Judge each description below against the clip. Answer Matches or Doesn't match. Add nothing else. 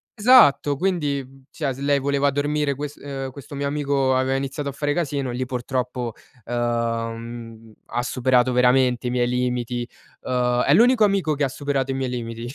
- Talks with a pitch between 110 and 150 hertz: Matches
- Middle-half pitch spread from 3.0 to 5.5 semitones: Doesn't match